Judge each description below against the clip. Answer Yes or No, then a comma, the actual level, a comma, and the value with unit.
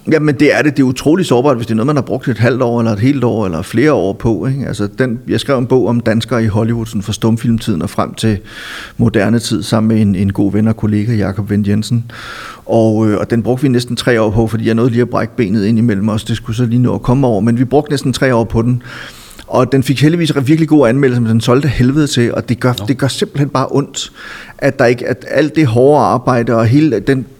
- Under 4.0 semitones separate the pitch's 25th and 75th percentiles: Yes, average, 2.9 semitones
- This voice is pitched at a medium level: No, low, 120 Hz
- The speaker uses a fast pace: Yes, fast, 270 wpm